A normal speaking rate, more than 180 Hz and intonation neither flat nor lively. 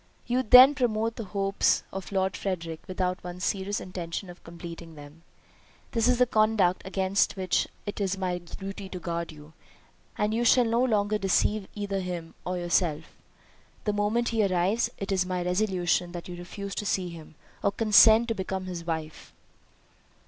Yes: average, 170 wpm; high, 190 Hz; average, 3.2 semitones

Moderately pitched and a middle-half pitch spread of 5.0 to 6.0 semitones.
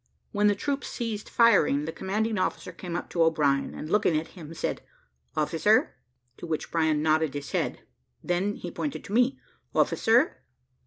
Yes: medium, 175 Hz; wide, 5.4 semitones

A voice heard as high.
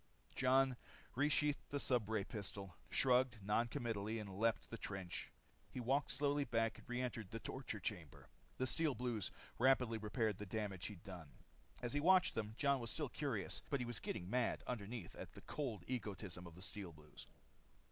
No: low, 115 Hz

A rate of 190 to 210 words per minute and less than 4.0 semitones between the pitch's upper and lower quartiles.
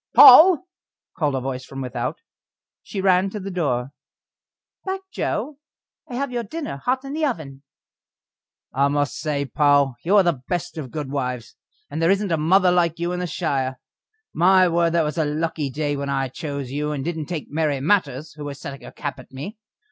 No: average, 195 wpm; average, 4.7 semitones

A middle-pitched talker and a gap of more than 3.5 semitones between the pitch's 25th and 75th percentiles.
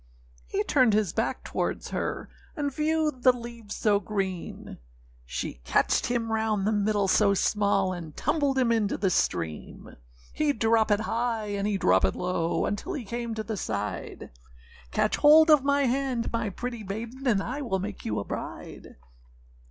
No: high, 220 Hz; average, 4.1 semitones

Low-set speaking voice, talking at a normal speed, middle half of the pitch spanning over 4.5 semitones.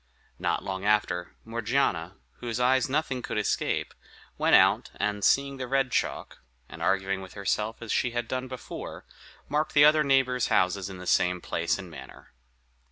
Yes: low, 115 Hz; average, 165 wpm; wide, 5.4 semitones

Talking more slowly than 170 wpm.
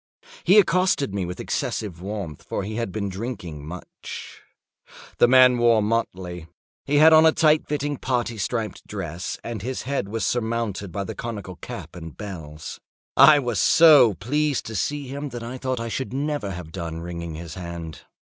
No: average, 175 wpm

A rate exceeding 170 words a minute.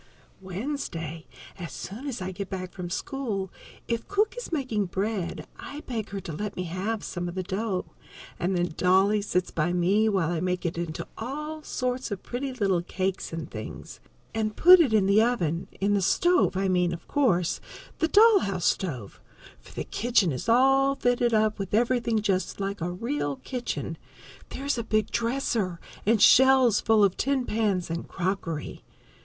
Yes: average, 185 wpm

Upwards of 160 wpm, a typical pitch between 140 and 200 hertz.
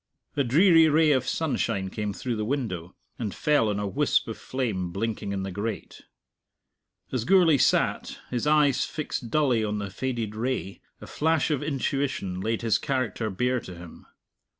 No: average, 170 wpm; low, 120 Hz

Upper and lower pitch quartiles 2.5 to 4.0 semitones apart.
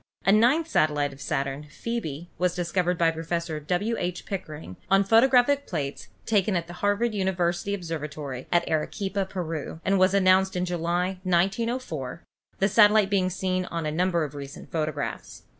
Yes: average, 3.7 semitones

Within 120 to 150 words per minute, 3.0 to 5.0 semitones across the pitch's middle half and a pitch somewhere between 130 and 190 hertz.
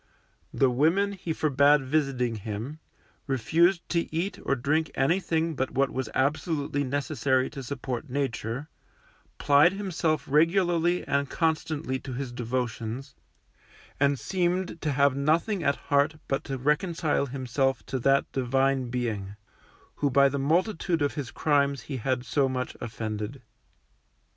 Yes: slow, 135 wpm; average, 3.4 semitones; medium, 140 Hz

